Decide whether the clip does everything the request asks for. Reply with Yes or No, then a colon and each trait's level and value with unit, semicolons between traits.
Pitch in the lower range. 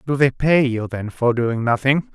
Yes: low, 125 Hz